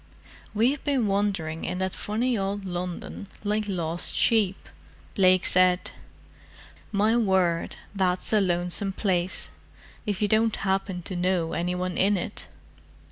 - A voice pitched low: No, high, 190 Hz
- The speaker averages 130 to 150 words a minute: Yes, slow, 135 wpm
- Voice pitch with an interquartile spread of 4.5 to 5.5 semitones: No, narrow, 2.4 semitones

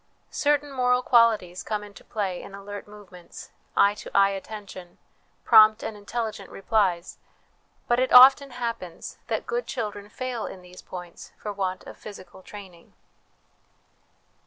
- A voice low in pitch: No, high, 205 Hz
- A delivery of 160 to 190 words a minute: No, slow, 135 wpm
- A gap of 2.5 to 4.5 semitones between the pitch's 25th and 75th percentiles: Yes, average, 3.9 semitones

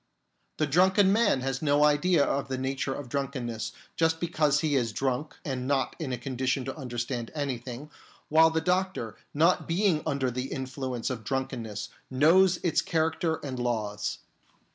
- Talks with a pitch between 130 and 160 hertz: Yes, medium, 140 Hz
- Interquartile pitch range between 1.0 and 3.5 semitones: No, average, 4.0 semitones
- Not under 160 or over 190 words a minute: Yes, average, 165 wpm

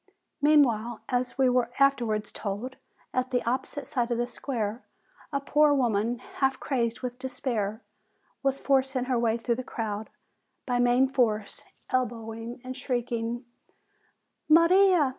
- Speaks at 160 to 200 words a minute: No, slow, 135 wpm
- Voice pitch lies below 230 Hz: No, high, 245 Hz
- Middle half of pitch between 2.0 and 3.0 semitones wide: Yes, narrow, 2.6 semitones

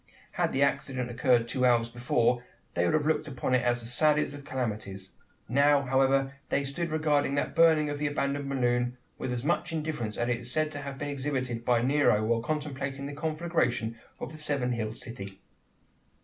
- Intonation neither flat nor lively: Yes, average, 3.3 semitones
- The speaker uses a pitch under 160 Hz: Yes, low, 135 Hz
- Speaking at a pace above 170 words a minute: Yes, average, 190 wpm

